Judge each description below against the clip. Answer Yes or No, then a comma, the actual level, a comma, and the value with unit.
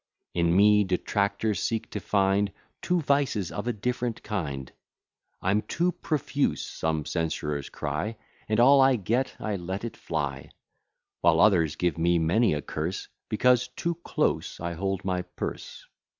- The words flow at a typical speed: Yes, average, 150 wpm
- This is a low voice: Yes, low, 100 Hz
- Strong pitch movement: Yes, wide, 5.7 semitones